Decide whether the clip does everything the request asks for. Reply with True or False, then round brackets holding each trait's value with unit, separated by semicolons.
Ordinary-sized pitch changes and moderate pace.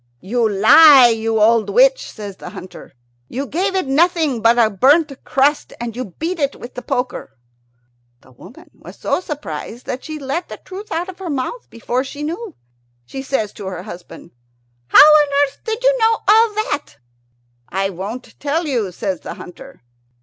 False (6.9 semitones; 180 wpm)